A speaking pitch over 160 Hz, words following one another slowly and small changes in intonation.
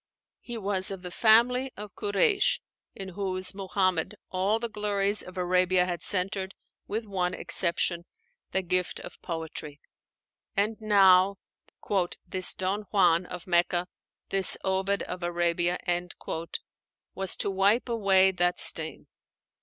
Yes: high, 190 Hz; slow, 125 wpm; narrow, 2.2 semitones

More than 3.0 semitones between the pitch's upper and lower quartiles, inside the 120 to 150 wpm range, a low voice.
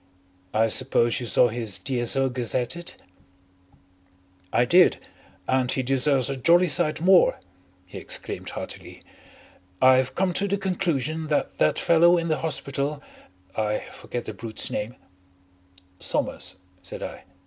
Yes: wide, 5.6 semitones; slow, 135 wpm; low, 130 Hz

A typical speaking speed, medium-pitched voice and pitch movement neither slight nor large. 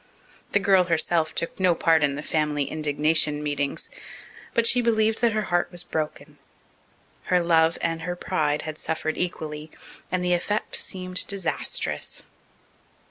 Yes: average, 145 wpm; medium, 165 Hz; average, 3.0 semitones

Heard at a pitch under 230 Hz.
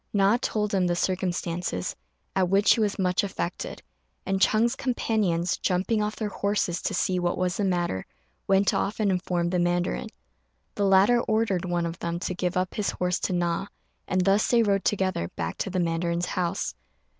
Yes: medium, 185 Hz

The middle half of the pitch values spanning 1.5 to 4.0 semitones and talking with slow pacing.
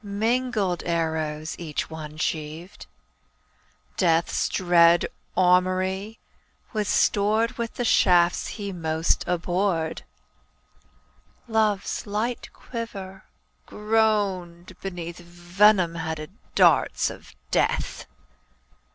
Yes: average, 3.7 semitones; slow, 80 wpm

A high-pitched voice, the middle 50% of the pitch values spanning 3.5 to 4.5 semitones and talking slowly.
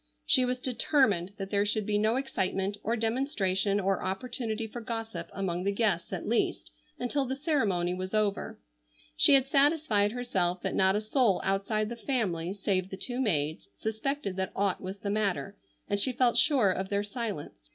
No: high, 210 Hz; average, 4.2 semitones; average, 180 wpm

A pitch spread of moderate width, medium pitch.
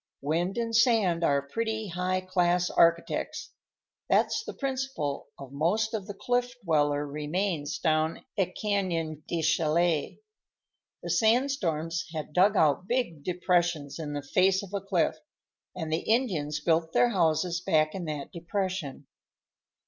Yes: average, 4.3 semitones; medium, 175 Hz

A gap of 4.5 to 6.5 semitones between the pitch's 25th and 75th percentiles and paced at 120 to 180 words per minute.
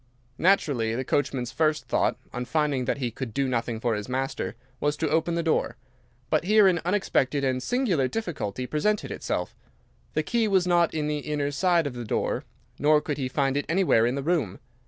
No: average, 5.0 semitones; average, 200 wpm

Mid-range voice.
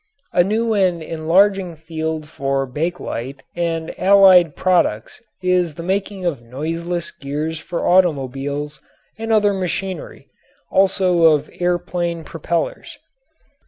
Yes: medium, 170 Hz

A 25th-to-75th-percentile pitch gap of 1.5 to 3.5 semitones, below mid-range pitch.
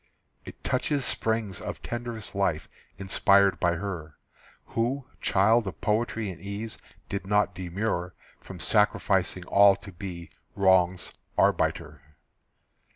Yes: average, 3.1 semitones; low, 100 Hz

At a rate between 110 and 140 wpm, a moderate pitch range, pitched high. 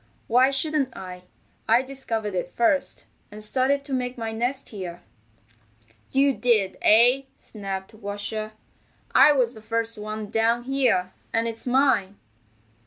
Yes: slow, 135 wpm; average, 3.8 semitones; high, 230 Hz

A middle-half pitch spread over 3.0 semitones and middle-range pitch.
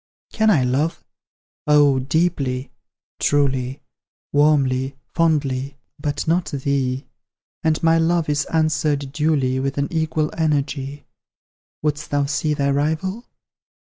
No: narrow, 2.5 semitones; medium, 145 Hz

